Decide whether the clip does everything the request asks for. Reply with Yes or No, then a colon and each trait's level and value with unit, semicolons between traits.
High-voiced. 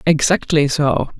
No: medium, 155 Hz